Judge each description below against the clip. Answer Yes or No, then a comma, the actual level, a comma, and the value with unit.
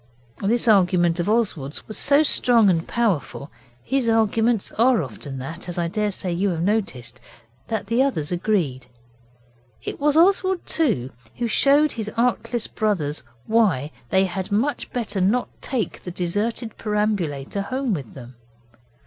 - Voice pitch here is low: No, high, 205 Hz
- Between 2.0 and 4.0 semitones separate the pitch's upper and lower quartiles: No, wide, 5.6 semitones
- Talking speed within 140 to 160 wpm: Yes, average, 145 wpm